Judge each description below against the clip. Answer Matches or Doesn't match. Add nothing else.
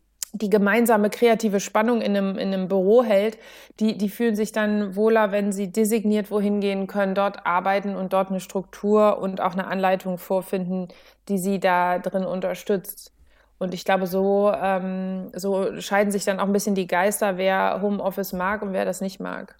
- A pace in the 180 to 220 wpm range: Matches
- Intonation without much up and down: Matches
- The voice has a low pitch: Doesn't match